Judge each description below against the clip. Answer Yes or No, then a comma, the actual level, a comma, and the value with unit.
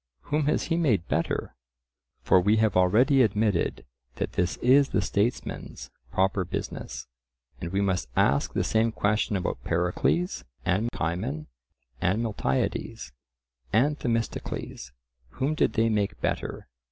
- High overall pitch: No, low, 105 Hz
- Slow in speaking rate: Yes, slow, 130 wpm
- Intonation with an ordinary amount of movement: Yes, average, 4.7 semitones